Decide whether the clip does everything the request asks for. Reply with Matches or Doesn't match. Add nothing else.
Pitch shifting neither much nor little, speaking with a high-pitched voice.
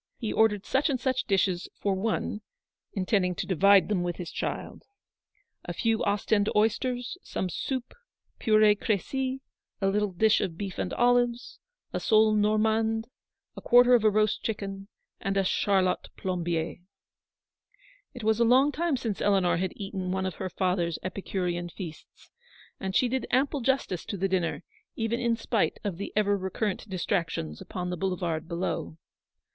Matches